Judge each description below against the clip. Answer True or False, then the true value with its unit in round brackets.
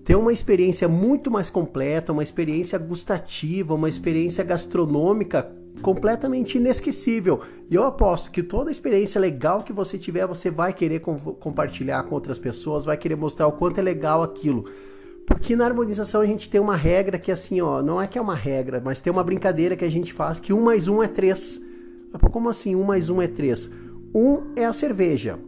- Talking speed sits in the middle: False (205 wpm)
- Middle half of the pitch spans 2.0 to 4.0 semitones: False (4.7 semitones)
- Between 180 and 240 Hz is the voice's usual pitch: True (185 Hz)